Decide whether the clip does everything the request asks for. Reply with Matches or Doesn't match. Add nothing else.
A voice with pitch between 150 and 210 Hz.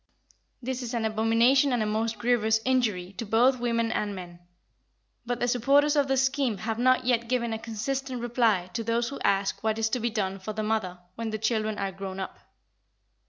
Doesn't match